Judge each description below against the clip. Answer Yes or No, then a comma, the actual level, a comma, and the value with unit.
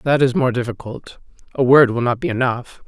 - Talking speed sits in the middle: No, fast, 210 wpm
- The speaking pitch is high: No, medium, 140 Hz